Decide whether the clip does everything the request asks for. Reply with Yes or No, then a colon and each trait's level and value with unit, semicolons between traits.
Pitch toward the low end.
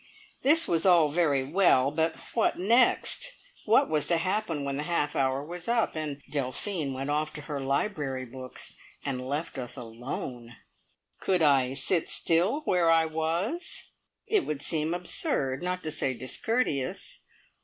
No: medium, 155 Hz